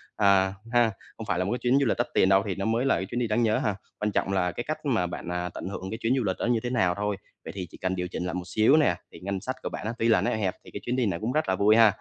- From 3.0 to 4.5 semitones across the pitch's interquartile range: Yes, average, 4.1 semitones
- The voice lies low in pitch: Yes, low, 105 Hz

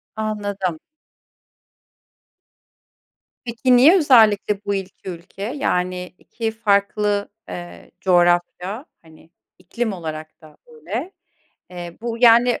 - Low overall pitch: No, high, 200 Hz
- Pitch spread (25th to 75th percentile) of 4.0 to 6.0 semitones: Yes, average, 4.5 semitones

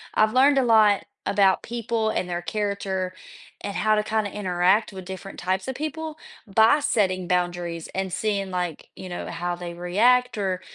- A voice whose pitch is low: No, high, 195 Hz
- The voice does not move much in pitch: No, average, 3.4 semitones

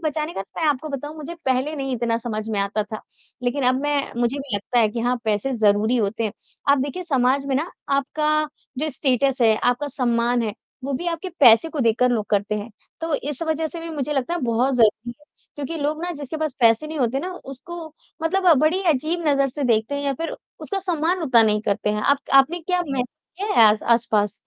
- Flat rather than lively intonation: No, average, 4.9 semitones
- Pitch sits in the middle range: No, very high, 270 Hz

